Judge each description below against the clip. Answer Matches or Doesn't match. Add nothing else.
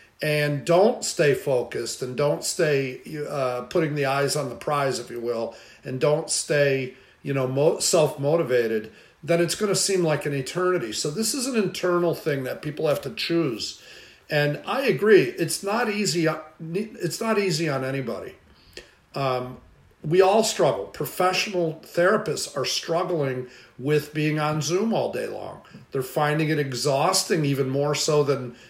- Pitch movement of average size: Matches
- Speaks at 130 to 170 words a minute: Matches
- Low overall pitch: Doesn't match